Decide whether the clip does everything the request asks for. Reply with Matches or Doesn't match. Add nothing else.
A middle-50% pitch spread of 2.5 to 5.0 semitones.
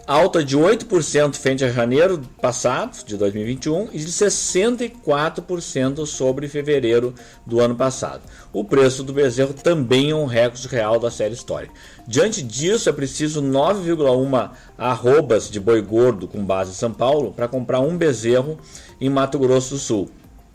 Matches